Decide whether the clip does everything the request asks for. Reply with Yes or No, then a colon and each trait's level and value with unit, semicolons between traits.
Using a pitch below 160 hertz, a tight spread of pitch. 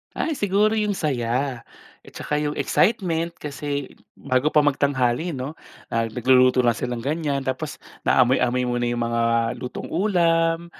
No: medium, 140 Hz; average, 4.9 semitones